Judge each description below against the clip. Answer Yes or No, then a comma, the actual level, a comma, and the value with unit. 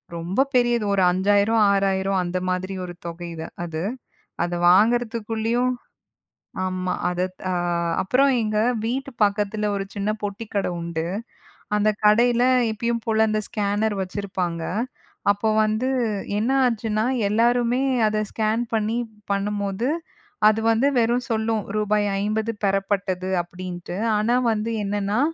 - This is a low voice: No, high, 210 Hz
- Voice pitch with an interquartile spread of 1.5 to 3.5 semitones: Yes, average, 2.8 semitones